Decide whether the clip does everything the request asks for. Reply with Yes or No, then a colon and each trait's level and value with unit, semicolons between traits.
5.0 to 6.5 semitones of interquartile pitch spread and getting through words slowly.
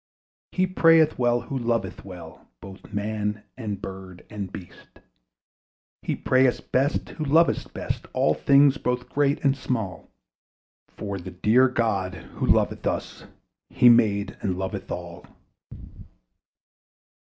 Yes: wide, 5.4 semitones; slow, 125 wpm